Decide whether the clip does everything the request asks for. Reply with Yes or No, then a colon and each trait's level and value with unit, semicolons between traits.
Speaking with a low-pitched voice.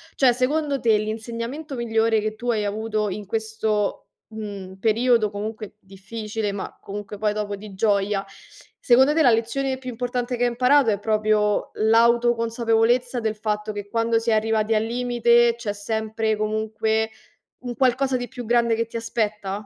No: high, 225 Hz